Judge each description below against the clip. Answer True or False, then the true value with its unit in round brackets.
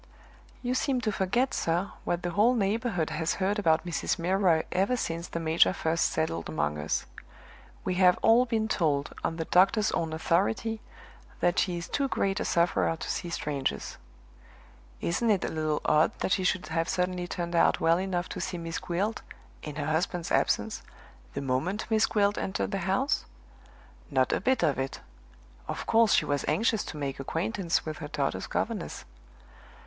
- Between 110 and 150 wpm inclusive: False (175 wpm)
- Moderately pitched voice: True (175 Hz)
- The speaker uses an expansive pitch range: False (4.2 semitones)